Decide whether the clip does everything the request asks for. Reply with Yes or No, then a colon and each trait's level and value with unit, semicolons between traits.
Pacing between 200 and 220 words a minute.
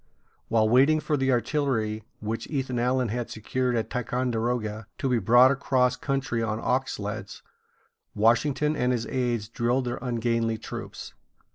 No: average, 145 wpm